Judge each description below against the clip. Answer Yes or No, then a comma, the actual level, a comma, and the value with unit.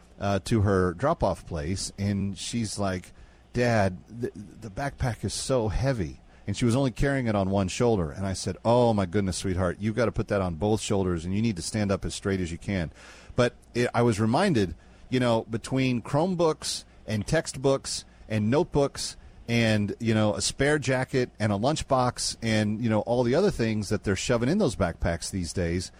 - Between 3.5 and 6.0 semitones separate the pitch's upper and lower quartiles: Yes, average, 4.0 semitones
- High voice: No, low, 105 Hz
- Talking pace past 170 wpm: Yes, average, 200 wpm